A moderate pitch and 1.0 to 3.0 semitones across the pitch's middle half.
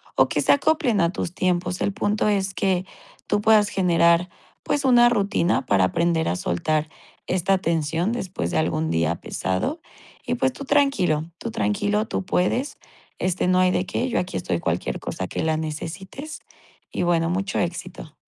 No: medium, 180 Hz; average, 4.5 semitones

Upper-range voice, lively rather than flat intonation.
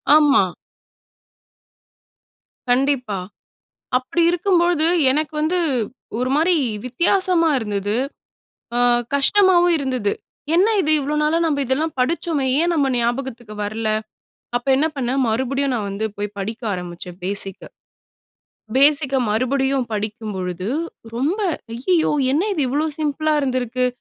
Yes: very high, 270 Hz; wide, 5.7 semitones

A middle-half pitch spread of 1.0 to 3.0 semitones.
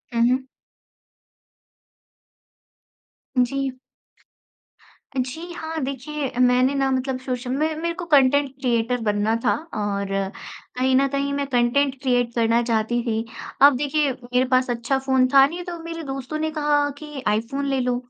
Yes: average, 2.7 semitones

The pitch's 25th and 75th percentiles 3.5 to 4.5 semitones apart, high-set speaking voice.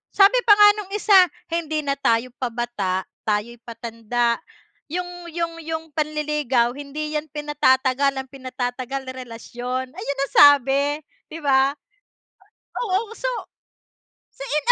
Yes: average, 4.1 semitones; very high, 275 Hz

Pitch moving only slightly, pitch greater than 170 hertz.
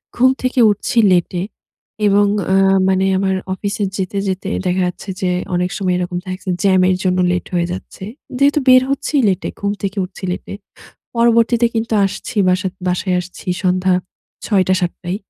Yes: narrow, 2.2 semitones; high, 190 Hz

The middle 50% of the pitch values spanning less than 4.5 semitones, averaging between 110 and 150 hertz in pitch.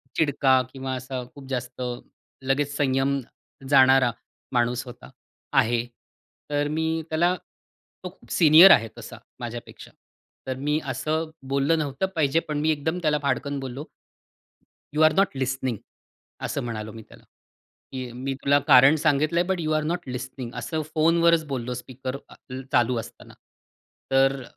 Yes: average, 3.3 semitones; medium, 140 Hz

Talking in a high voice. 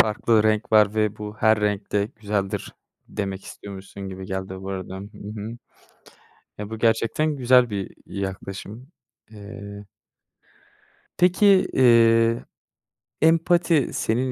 No: low, 105 Hz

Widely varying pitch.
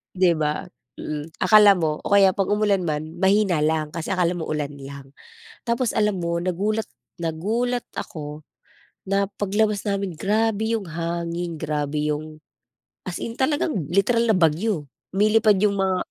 No: average, 5.0 semitones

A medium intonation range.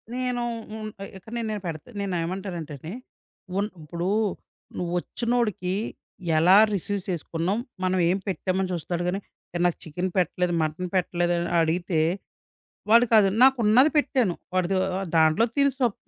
Yes: average, 3.8 semitones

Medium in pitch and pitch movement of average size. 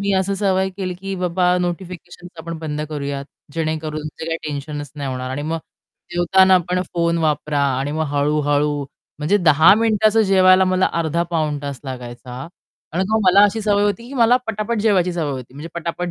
Yes: medium, 170 Hz; average, 4.2 semitones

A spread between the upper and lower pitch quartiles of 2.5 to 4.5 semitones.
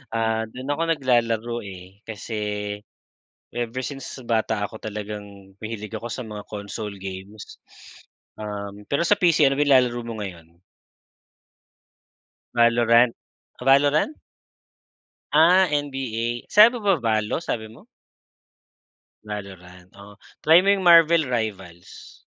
No: average, 4.9 semitones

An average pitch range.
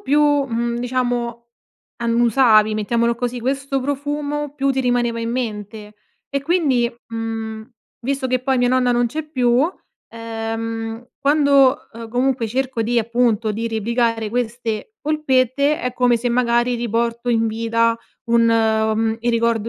No: narrow, 2.2 semitones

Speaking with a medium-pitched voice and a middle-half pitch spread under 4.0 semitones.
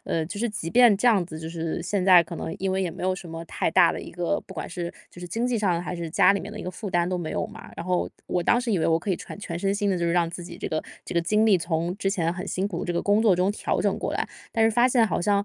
Yes: medium, 180 Hz; average, 3.1 semitones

